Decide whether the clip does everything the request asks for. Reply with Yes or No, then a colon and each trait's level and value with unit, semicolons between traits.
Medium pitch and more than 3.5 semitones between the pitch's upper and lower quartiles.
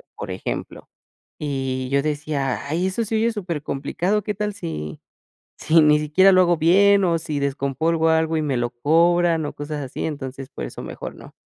Yes: medium, 155 Hz; average, 3.9 semitones